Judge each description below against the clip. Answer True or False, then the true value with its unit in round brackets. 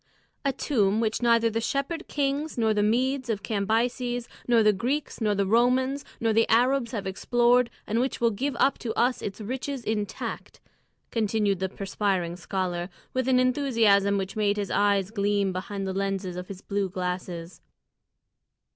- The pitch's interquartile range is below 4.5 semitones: True (4.0 semitones)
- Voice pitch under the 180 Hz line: False (220 Hz)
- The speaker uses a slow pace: False (165 wpm)